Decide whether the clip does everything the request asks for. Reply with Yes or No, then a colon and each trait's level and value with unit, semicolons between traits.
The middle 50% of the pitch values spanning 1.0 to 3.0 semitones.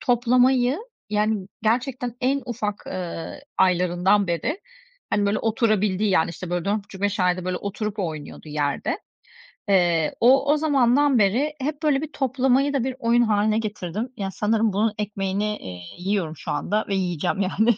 No: average, 4.8 semitones